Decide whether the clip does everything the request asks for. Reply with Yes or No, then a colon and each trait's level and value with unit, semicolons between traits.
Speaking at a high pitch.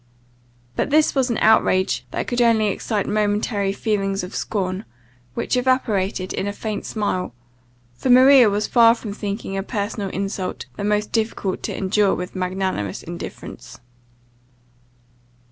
Yes: high, 205 Hz